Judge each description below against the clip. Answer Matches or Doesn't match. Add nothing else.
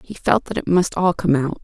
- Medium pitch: Matches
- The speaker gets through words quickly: Matches